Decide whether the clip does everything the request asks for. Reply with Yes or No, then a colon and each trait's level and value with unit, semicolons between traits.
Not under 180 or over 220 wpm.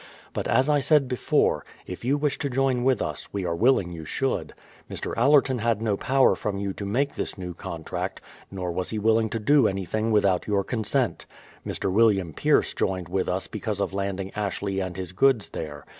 Yes: average, 200 wpm